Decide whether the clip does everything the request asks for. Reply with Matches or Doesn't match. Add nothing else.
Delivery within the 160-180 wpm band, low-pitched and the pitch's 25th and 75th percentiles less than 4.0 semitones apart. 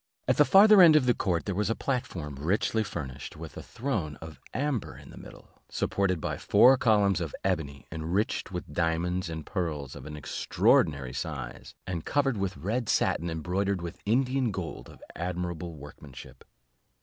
Doesn't match